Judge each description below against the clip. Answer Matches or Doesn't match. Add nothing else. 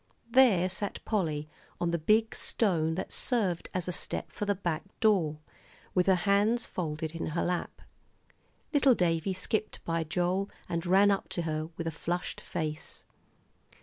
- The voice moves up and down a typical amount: Matches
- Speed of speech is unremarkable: Matches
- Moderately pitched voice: Matches